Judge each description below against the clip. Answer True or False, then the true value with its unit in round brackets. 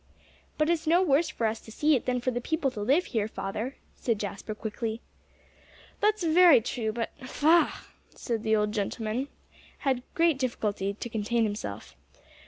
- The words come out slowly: False (170 wpm)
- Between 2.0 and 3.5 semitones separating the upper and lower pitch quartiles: False (5.6 semitones)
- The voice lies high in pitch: True (240 Hz)